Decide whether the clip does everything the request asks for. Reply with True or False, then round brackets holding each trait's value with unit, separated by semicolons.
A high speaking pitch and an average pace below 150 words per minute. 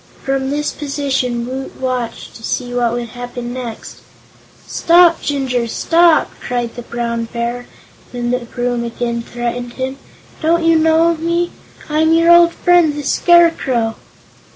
True (255 Hz; 140 wpm)